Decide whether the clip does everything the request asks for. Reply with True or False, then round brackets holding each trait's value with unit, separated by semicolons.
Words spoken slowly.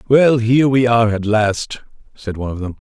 False (210 wpm)